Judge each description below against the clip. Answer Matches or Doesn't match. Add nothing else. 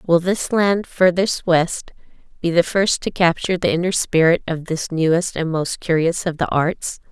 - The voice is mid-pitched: Matches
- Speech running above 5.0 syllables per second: Doesn't match